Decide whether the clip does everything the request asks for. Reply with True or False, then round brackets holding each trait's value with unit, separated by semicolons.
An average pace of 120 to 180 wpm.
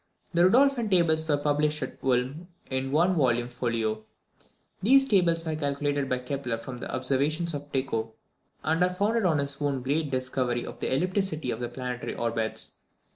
True (170 wpm)